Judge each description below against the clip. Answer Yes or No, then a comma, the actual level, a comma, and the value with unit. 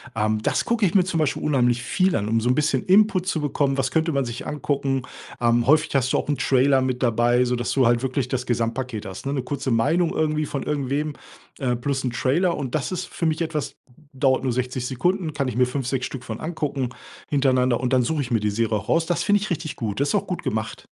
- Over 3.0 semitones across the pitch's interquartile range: Yes, average, 3.8 semitones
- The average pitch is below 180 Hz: Yes, low, 135 Hz